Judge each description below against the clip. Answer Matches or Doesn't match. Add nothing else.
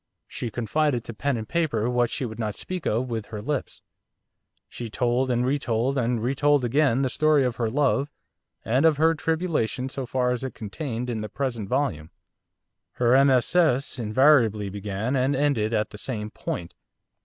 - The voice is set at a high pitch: Doesn't match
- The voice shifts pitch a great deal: Doesn't match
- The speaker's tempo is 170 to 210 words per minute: Matches